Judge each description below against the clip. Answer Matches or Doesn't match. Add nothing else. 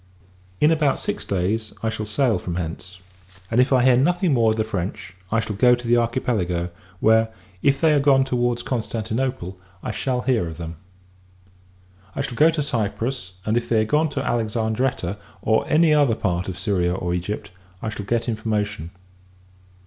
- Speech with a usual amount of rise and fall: Matches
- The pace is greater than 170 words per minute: Matches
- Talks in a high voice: Doesn't match